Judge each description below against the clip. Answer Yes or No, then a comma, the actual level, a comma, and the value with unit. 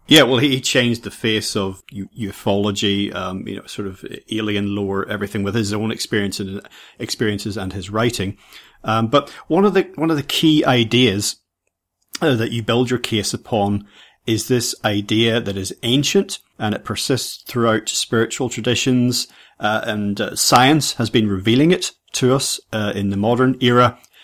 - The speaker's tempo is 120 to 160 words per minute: No, average, 175 wpm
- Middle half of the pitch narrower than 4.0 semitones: Yes, average, 3.4 semitones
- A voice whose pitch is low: Yes, low, 110 Hz